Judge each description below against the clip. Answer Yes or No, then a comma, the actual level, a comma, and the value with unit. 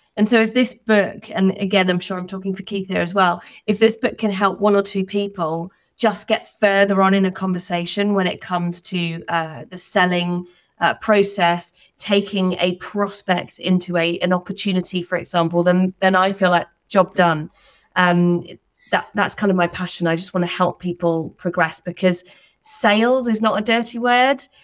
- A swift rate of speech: No, average, 190 wpm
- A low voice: No, medium, 185 Hz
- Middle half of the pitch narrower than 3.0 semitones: Yes, narrow, 2.4 semitones